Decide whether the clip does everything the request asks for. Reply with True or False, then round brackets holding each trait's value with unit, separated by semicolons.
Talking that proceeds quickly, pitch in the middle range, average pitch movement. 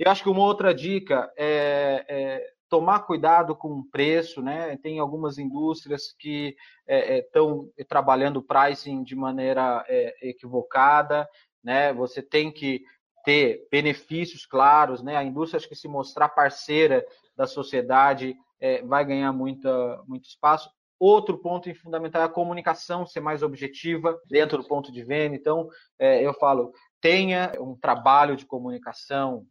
False (150 wpm; 150 Hz; 3.6 semitones)